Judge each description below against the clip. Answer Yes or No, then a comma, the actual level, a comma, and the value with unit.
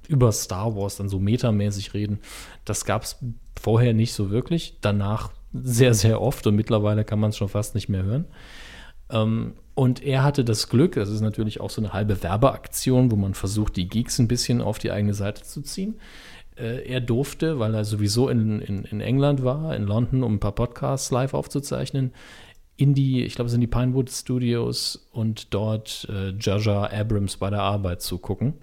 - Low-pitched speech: Yes, low, 110 Hz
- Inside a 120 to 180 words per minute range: No, fast, 190 wpm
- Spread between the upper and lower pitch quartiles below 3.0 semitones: No, average, 3.6 semitones